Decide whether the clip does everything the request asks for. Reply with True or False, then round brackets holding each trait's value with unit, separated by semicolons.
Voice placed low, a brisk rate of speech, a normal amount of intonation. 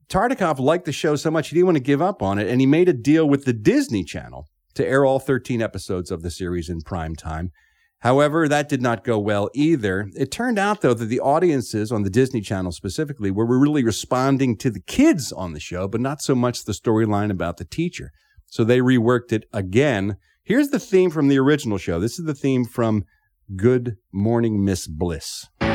False (120 Hz; 215 wpm; 6.7 semitones)